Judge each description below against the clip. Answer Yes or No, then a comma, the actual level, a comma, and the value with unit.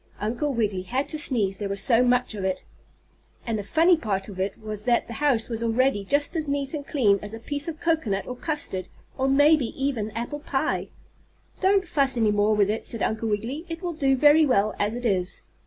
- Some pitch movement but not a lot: No, wide, 5.7 semitones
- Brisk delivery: Yes, fast, 220 wpm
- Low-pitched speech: No, high, 240 Hz